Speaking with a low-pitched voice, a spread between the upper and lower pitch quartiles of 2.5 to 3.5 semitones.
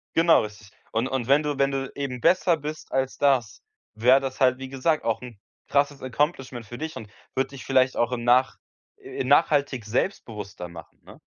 Yes: low, 130 Hz; average, 3.2 semitones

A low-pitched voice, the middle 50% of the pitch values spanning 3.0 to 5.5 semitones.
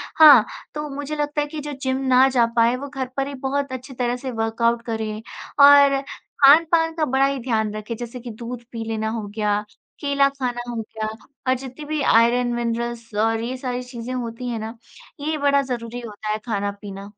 No: high, 245 Hz; average, 3.4 semitones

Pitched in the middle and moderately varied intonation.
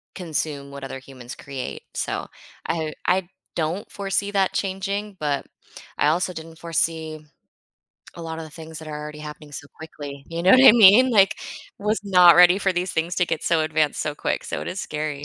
Yes: medium, 165 Hz; average, 3.8 semitones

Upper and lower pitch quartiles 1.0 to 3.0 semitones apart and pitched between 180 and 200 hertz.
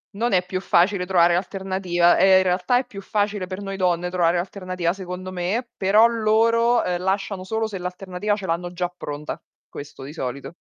Yes: narrow, 2.4 semitones; medium, 185 Hz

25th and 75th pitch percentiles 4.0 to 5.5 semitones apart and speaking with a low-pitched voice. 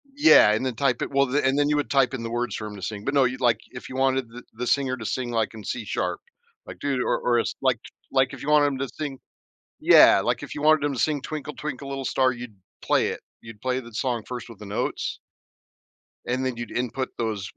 No: average, 2.7 semitones; low, 130 Hz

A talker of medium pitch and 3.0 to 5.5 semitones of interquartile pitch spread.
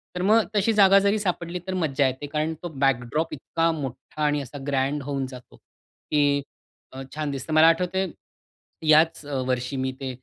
Yes: medium, 150 Hz; average, 4.1 semitones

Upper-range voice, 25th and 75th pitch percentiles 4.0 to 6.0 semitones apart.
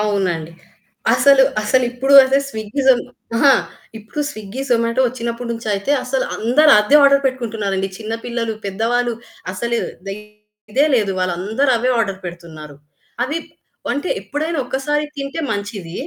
Yes: high, 235 Hz; average, 4.8 semitones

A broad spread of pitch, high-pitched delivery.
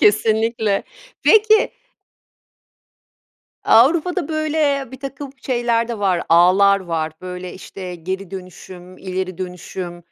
Yes: wide, 6.4 semitones; high, 200 Hz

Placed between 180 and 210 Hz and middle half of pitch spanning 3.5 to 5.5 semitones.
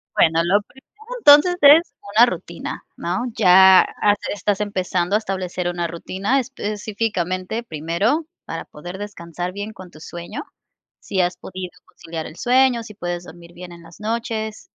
Yes: high, 190 Hz; average, 4.1 semitones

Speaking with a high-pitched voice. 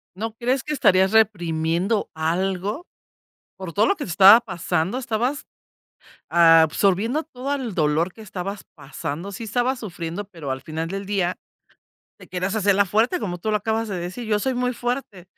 Yes: high, 200 Hz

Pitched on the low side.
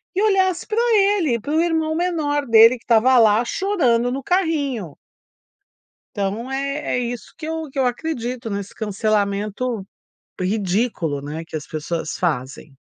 No: high, 245 Hz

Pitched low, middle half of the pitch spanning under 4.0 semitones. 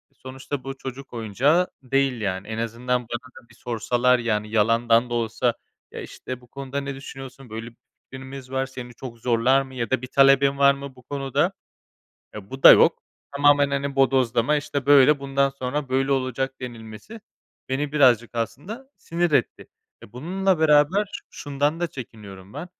Yes: low, 130 Hz; average, 2.7 semitones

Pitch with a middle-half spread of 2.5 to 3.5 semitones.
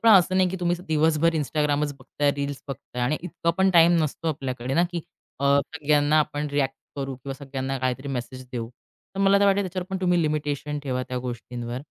No: average, 4.1 semitones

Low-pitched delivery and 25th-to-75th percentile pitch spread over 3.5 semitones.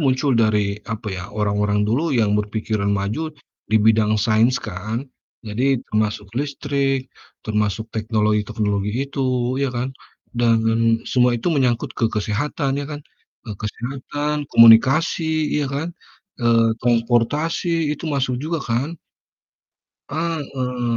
Yes: low, 120 Hz; average, 4.5 semitones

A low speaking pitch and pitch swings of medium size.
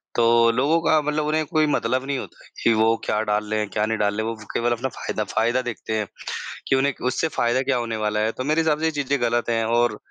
Yes: low, 120 Hz; average, 4.2 semitones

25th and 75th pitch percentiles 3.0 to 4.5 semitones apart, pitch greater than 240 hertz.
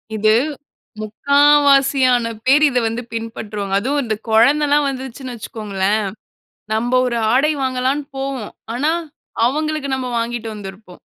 Yes: average, 3.9 semitones; very high, 250 Hz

